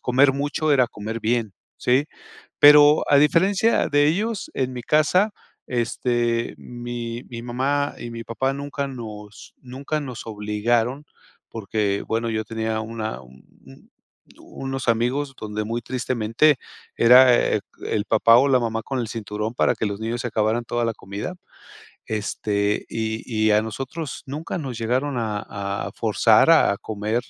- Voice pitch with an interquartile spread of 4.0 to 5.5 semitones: No, average, 3.6 semitones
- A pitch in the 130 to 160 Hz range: No, low, 120 Hz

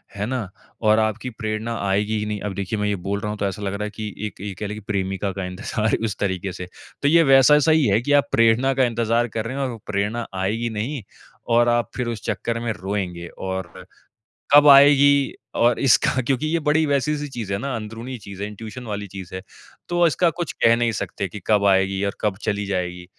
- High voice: No, low, 110 Hz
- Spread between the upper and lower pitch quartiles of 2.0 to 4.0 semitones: No, average, 4.4 semitones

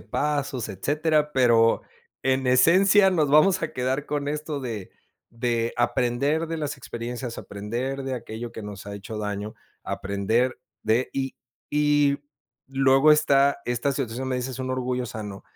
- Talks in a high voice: No, low, 130 Hz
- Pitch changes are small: No, average, 3.9 semitones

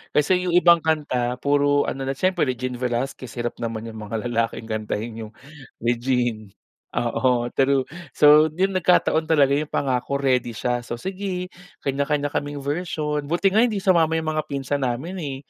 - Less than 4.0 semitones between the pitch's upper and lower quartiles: No, average, 4.6 semitones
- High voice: No, medium, 140 Hz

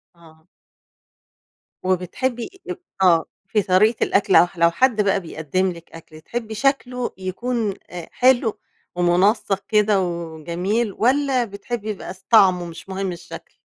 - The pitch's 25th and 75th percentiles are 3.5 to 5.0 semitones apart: Yes, average, 4.7 semitones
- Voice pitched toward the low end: No, high, 195 Hz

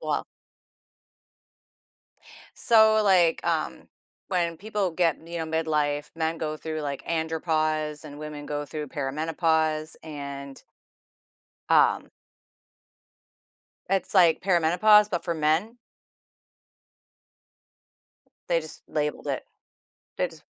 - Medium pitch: Yes, medium, 160 Hz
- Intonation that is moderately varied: No, narrow, 2.3 semitones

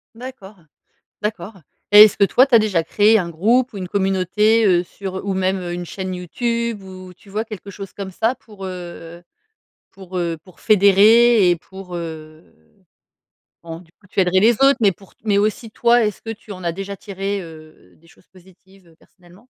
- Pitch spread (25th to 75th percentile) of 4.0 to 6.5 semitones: No, average, 3.2 semitones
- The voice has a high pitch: Yes, high, 195 Hz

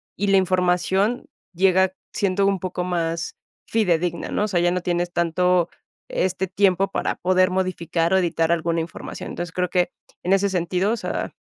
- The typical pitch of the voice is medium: Yes, medium, 180 Hz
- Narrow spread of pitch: Yes, narrow, 1.6 semitones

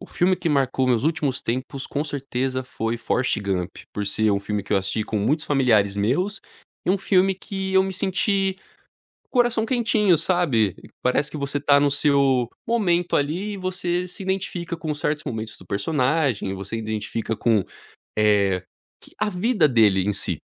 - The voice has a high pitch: No, medium, 140 Hz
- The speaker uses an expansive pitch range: Yes, wide, 8.5 semitones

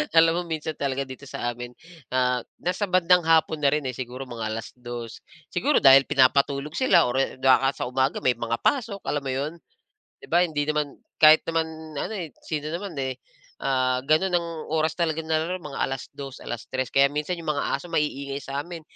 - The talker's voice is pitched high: No, medium, 145 Hz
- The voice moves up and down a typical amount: Yes, average, 3.7 semitones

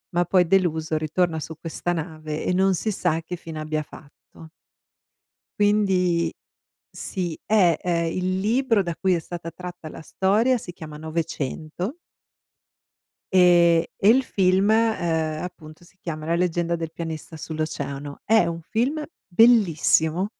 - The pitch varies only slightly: No, average, 3.0 semitones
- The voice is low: No, medium, 170 Hz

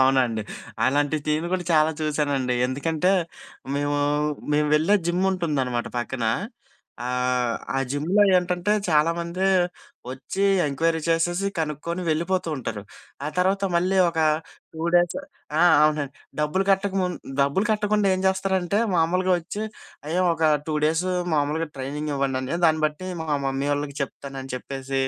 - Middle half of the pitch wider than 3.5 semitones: Yes, average, 4.3 semitones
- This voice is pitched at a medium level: Yes, medium, 155 Hz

